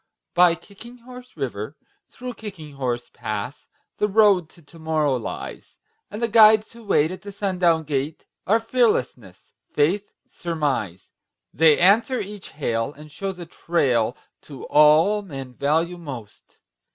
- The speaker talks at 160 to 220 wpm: No, average, 140 wpm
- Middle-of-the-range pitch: Yes, medium, 165 Hz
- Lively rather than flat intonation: Yes, wide, 6.5 semitones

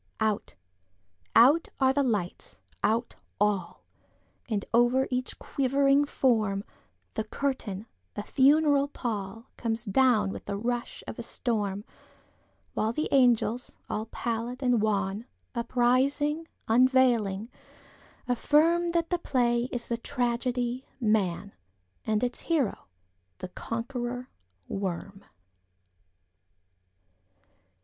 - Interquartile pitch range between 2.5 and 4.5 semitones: Yes, average, 4.0 semitones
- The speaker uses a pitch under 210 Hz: No, high, 235 Hz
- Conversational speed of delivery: No, slow, 85 wpm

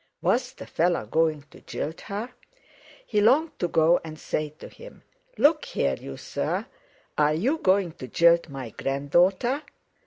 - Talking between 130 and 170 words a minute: Yes, average, 160 wpm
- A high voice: No, medium, 170 Hz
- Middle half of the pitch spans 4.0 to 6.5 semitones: Yes, wide, 5.4 semitones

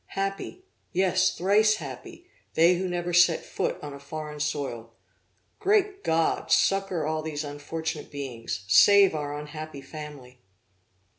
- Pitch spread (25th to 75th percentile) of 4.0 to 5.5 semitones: Yes, average, 4.4 semitones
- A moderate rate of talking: No, slow, 130 wpm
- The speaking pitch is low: No, medium, 155 Hz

